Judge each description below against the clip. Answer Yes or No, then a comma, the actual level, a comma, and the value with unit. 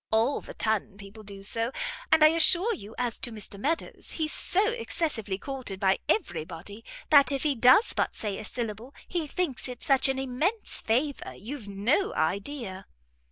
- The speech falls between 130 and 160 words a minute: No, average, 175 wpm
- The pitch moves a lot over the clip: Yes, wide, 6.8 semitones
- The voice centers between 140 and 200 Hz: No, high, 245 Hz